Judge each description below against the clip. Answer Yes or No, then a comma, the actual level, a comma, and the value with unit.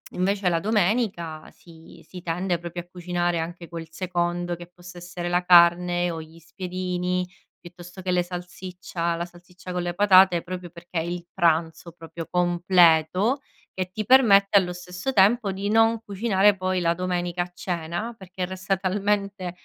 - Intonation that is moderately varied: No, narrow, 1.6 semitones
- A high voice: No, medium, 180 Hz